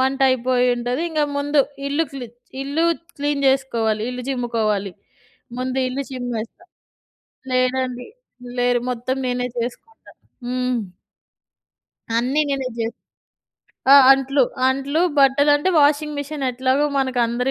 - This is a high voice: Yes, very high, 260 Hz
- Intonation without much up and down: Yes, narrow, 2.3 semitones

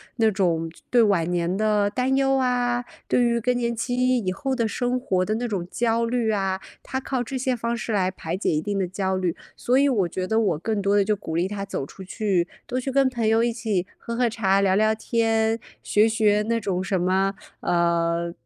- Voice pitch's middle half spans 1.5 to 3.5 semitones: No, average, 4.2 semitones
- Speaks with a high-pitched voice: Yes, high, 215 Hz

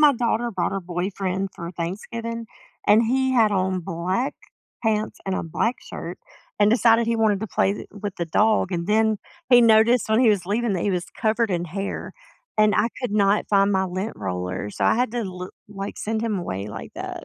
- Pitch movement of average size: Yes, average, 3.6 semitones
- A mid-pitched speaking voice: No, high, 205 Hz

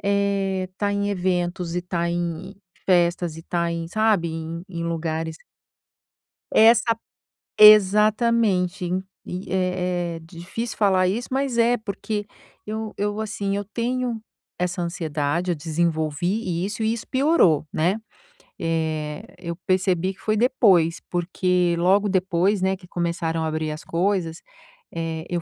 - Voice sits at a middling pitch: Yes, medium, 180 Hz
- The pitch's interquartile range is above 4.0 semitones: No, average, 3.4 semitones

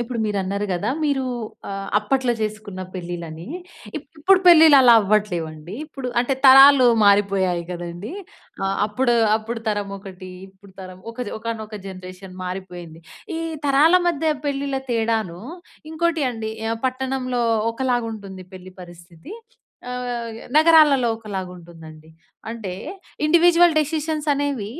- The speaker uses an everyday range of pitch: No, wide, 6.3 semitones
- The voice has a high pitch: Yes, high, 220 Hz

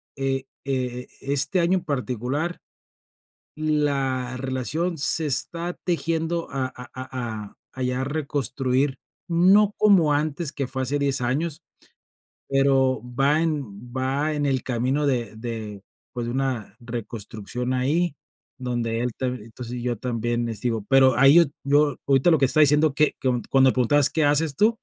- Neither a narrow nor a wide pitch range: Yes, average, 3.2 semitones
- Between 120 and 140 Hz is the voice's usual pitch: Yes, low, 135 Hz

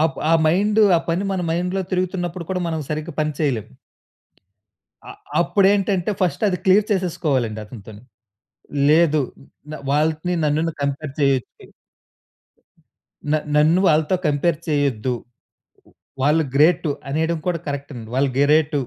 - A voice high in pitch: No, medium, 155 Hz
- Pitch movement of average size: Yes, average, 3.8 semitones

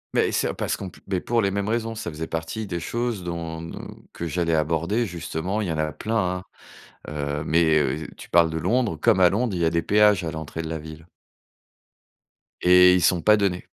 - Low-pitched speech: Yes, very low, 85 Hz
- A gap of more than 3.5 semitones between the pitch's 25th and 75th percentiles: Yes, average, 3.9 semitones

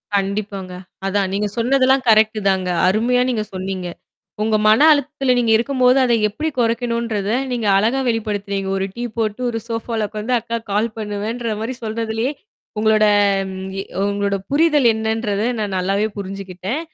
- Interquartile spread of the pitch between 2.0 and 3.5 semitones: Yes, average, 2.9 semitones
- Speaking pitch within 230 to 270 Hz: No, high, 220 Hz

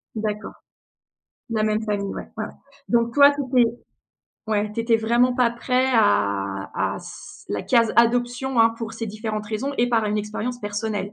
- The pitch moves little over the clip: Yes, narrow, 2.1 semitones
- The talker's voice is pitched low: No, high, 225 Hz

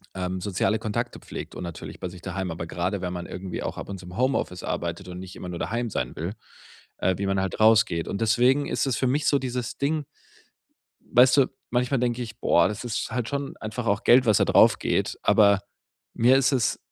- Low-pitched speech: Yes, low, 110 Hz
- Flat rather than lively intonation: No, average, 5.3 semitones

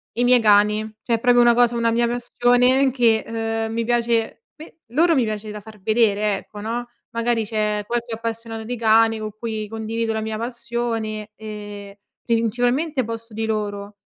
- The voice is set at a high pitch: Yes, high, 225 Hz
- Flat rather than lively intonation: Yes, narrow, 1.9 semitones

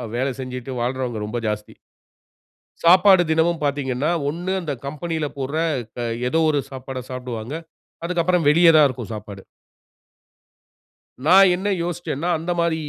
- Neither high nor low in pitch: Yes, medium, 145 Hz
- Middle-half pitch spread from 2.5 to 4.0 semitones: No, average, 5.0 semitones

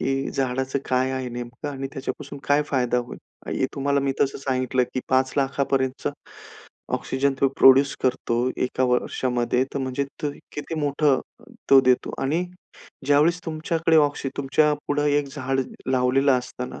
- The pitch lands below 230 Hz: Yes, low, 135 Hz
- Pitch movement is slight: Yes, narrow, 1.8 semitones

